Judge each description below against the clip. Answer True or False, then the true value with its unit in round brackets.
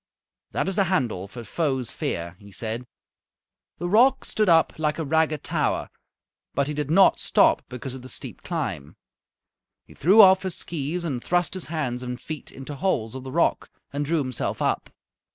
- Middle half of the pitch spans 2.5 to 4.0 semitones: False (5.6 semitones)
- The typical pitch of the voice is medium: True (150 Hz)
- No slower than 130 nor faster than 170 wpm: False (185 wpm)